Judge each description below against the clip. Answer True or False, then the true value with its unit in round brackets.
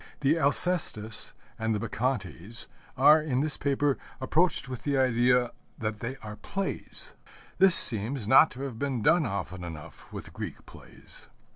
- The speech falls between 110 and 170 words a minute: True (150 wpm)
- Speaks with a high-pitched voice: False (130 Hz)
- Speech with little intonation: False (4.5 semitones)